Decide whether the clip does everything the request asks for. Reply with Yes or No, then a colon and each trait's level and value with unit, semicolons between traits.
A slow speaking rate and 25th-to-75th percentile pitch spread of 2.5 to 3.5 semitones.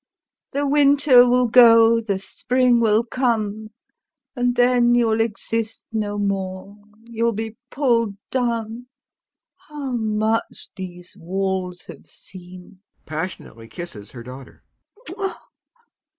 Yes: slow, 90 wpm; average, 3.2 semitones